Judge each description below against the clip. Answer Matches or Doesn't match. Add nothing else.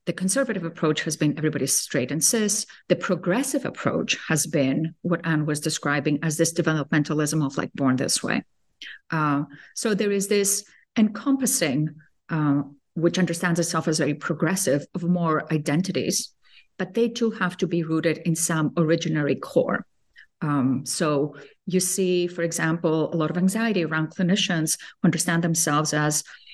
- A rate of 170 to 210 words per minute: Doesn't match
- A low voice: Doesn't match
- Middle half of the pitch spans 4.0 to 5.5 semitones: Doesn't match